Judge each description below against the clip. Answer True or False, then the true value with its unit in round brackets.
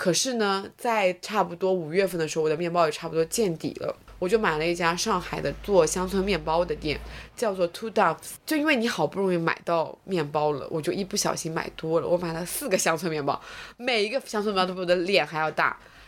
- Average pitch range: True (3.7 semitones)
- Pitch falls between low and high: True (175 Hz)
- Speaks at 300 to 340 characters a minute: False (355 characters per minute)